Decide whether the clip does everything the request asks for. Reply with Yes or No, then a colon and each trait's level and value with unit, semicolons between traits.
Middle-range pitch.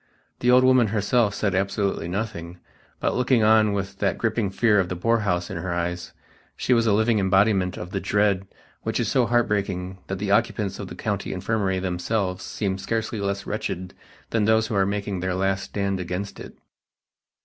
No: low, 100 Hz